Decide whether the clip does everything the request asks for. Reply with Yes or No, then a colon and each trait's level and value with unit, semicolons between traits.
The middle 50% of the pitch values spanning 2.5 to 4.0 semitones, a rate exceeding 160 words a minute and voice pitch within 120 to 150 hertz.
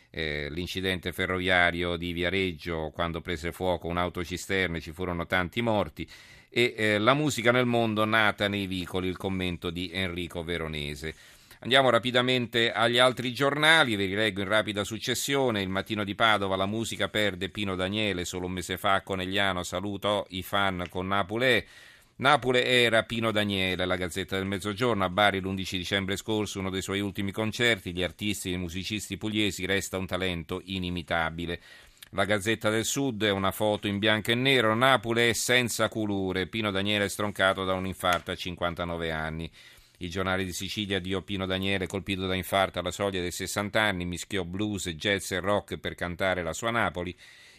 No: average, 2.9 semitones; fast, 170 wpm; very low, 95 Hz